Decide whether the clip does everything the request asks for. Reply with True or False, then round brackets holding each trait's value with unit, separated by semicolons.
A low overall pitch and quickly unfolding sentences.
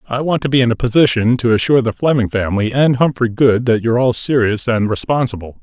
True (120 Hz; 225 wpm)